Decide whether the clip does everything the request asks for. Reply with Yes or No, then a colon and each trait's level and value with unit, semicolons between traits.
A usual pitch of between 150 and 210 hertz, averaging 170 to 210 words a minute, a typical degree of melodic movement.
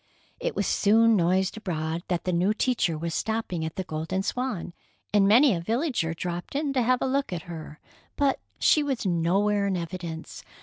No: high, 190 Hz; average, 185 wpm; wide, 5.7 semitones